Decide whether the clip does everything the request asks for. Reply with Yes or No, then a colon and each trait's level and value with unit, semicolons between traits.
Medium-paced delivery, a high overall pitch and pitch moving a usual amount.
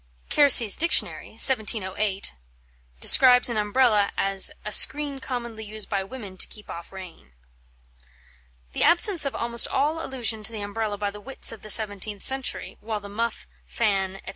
Yes: average, 160 wpm; high, 215 Hz; average, 3.8 semitones